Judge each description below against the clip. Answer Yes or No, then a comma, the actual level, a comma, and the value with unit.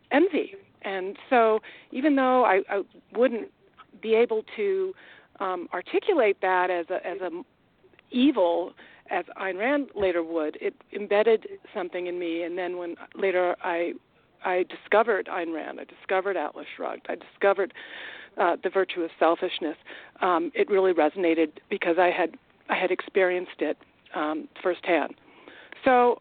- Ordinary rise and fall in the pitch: No, wide, 6.2 semitones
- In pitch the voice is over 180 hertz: Yes, high, 190 Hz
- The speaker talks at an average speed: Yes, average, 145 wpm